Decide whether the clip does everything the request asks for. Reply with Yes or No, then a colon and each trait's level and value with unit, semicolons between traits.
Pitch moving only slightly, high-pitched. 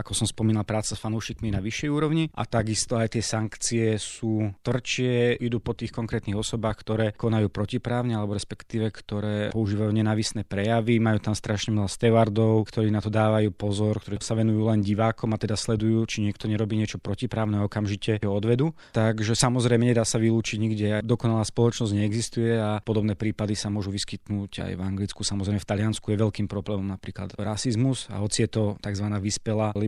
No: narrow, 1.6 semitones; low, 110 Hz